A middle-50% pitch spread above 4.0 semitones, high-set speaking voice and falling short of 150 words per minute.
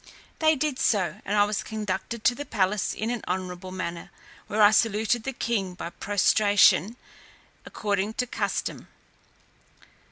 No: average, 3.5 semitones; high, 210 Hz; average, 140 wpm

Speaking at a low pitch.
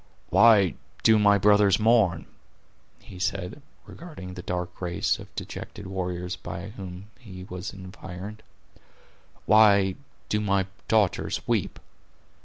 Yes: very low, 95 Hz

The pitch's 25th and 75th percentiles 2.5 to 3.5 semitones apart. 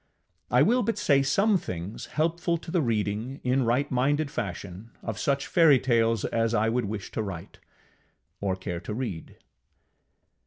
No: wide, 5.5 semitones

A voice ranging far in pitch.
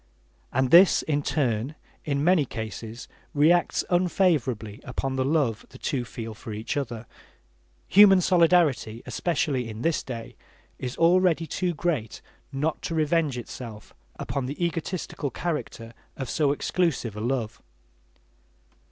Yes: wide, 6.0 semitones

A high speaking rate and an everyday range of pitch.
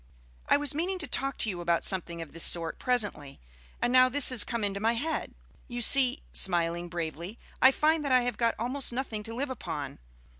No: fast, 210 wpm; wide, 7.1 semitones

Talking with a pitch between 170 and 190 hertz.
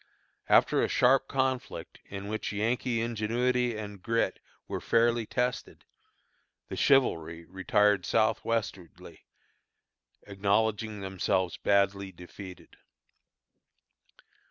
No: low, 105 Hz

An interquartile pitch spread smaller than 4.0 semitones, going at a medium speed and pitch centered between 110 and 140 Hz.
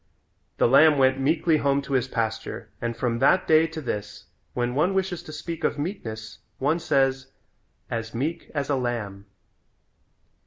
No: average, 5.0 semitones; average, 160 wpm; low, 135 Hz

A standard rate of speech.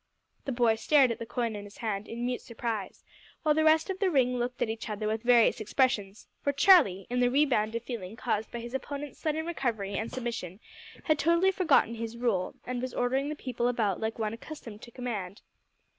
No: fast, 210 wpm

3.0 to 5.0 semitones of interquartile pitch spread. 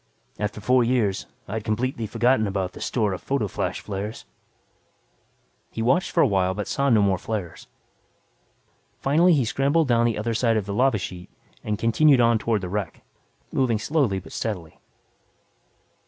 Yes: average, 4.1 semitones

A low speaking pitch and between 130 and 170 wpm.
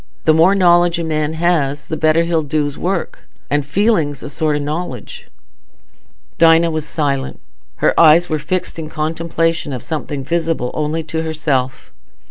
No: medium, 160 Hz; average, 155 wpm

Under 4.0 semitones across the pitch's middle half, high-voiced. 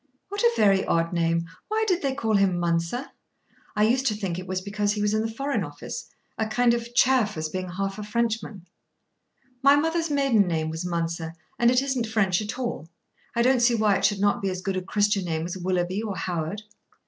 No: average, 4.9 semitones; high, 205 Hz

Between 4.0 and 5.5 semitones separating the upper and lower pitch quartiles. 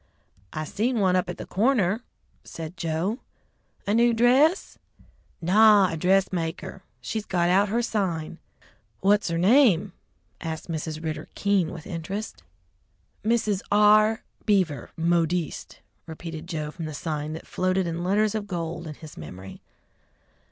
Yes: average, 4.4 semitones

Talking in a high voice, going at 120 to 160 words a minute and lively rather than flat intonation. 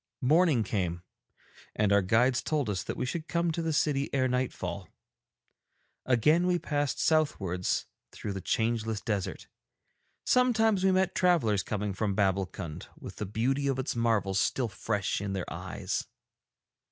No: low, 115 Hz; average, 150 wpm; wide, 7.4 semitones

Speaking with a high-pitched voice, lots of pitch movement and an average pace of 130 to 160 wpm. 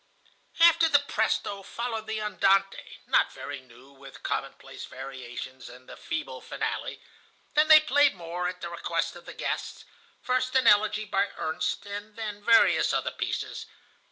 Yes: high, 205 Hz; wide, 7.2 semitones; average, 150 wpm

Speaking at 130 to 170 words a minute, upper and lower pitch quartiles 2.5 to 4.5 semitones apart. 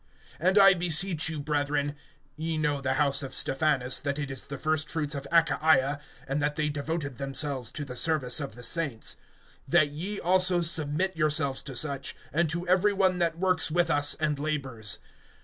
No: average, 185 wpm; average, 3.0 semitones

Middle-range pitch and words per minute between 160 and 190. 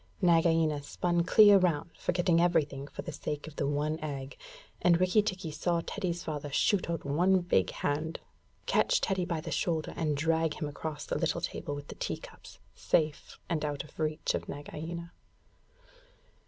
Yes: medium, 160 Hz; average, 170 wpm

